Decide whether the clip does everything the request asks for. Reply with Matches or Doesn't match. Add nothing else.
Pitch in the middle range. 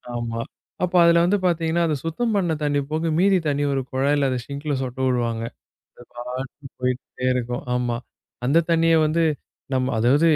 Matches